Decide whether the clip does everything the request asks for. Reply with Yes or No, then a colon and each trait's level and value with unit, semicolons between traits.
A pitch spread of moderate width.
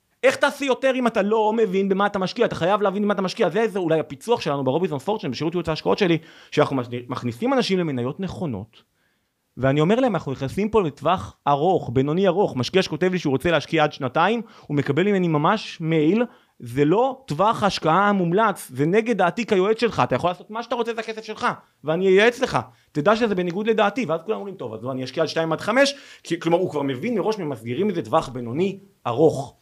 No: wide, 6.7 semitones